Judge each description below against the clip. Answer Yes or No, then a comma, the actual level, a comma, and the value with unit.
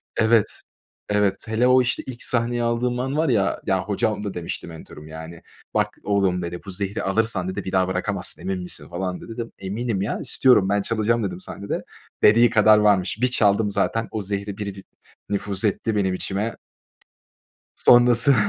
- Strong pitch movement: No, average, 3.4 semitones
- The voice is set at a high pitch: No, low, 105 Hz